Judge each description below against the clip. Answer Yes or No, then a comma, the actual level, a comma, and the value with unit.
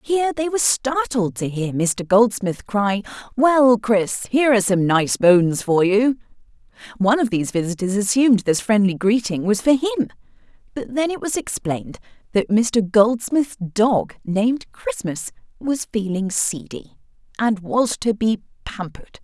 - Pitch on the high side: Yes, high, 220 Hz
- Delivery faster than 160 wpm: No, average, 150 wpm